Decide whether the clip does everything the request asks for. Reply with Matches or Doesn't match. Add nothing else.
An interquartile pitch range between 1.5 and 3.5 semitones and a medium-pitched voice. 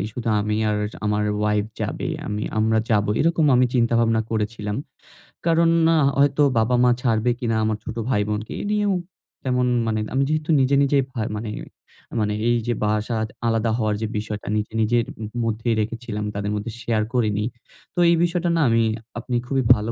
Doesn't match